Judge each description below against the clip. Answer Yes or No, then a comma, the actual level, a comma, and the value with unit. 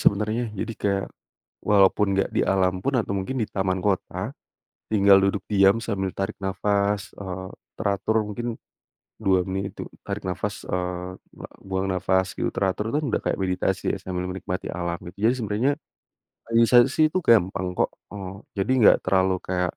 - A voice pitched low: Yes, very low, 95 Hz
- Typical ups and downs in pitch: No, narrow, 2.0 semitones